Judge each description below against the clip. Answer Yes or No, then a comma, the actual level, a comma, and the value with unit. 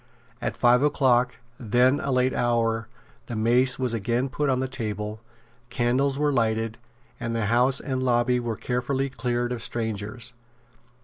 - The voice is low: Yes, low, 120 Hz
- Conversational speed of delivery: Yes, average, 150 wpm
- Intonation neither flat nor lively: No, narrow, 2.0 semitones